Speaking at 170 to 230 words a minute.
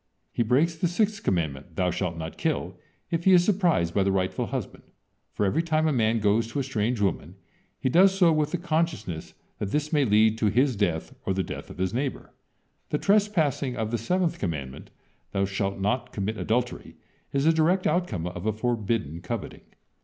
Yes: average, 195 wpm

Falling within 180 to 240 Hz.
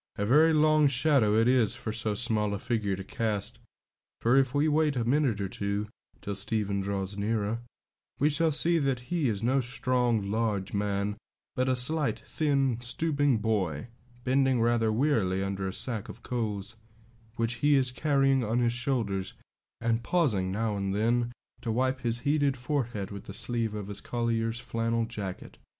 No: low, 115 Hz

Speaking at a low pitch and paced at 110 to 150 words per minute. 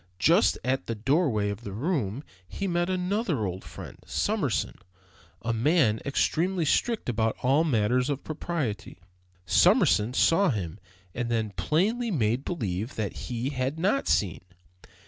Yes: low, 130 Hz; average, 140 wpm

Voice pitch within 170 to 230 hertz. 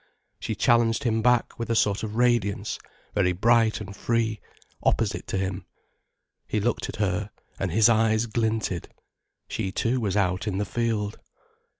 No: low, 110 Hz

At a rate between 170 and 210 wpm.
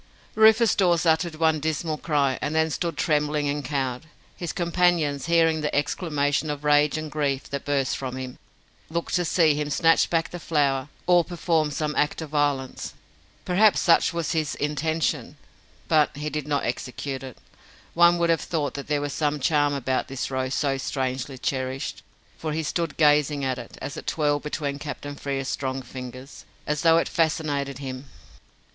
Yes: average, 175 wpm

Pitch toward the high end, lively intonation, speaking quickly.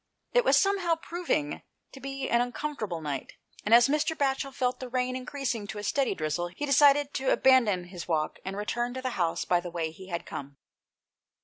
Yes: high, 245 Hz; wide, 7.6 semitones; fast, 210 wpm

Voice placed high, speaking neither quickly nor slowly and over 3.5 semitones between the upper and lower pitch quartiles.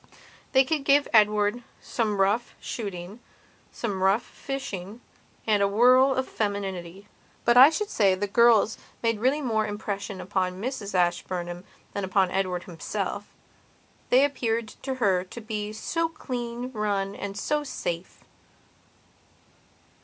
No: high, 210 Hz; slow, 130 wpm; average, 4.1 semitones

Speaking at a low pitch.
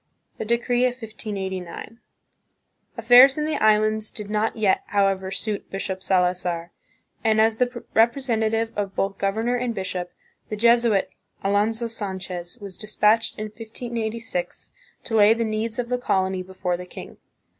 No: high, 215 Hz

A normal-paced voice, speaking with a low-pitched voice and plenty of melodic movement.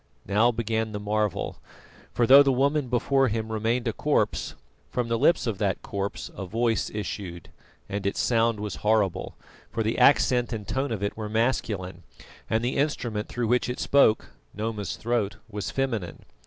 No: average, 170 wpm; low, 110 Hz; average, 2.8 semitones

